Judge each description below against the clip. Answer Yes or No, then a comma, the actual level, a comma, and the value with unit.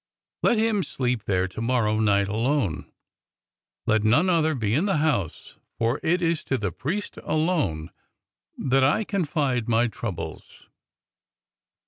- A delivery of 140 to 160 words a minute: Yes, average, 145 wpm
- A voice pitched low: Yes, low, 130 Hz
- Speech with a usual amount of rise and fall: No, wide, 6.7 semitones